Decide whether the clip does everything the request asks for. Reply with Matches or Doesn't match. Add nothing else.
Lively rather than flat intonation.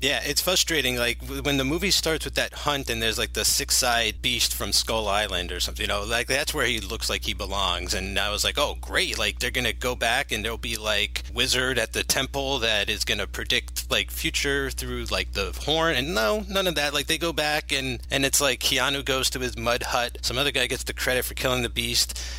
Matches